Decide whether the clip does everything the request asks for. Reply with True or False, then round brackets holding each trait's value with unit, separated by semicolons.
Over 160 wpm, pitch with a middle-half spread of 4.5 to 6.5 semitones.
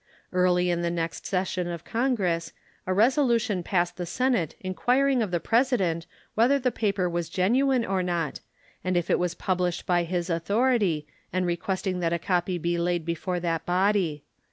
False (170 wpm; 3.6 semitones)